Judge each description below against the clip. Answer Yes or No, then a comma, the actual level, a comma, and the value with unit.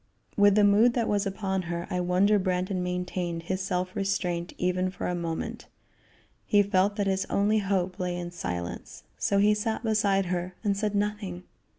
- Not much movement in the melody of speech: Yes, narrow, 2.2 semitones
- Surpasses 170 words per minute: Yes, average, 180 wpm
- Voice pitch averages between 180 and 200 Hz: Yes, high, 190 Hz